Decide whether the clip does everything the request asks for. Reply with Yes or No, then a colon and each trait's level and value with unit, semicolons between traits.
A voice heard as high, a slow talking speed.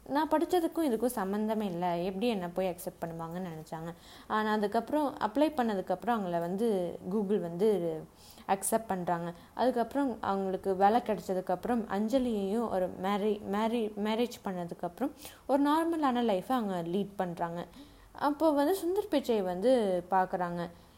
No: high, 210 Hz; average, 125 wpm